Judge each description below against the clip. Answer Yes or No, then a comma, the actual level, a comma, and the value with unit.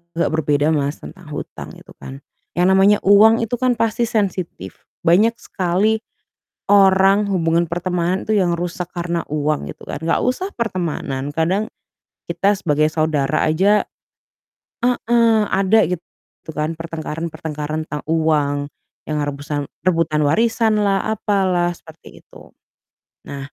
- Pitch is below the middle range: No, medium, 175 Hz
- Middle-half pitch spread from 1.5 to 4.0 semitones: No, average, 5.0 semitones